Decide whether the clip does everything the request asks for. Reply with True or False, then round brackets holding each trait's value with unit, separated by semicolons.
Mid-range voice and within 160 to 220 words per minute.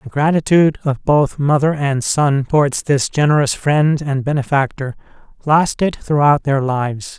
False (145 Hz; 140 wpm)